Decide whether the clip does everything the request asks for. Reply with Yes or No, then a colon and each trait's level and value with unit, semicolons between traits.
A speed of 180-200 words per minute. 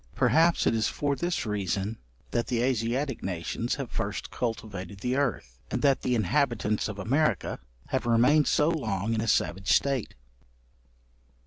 No: average, 150 wpm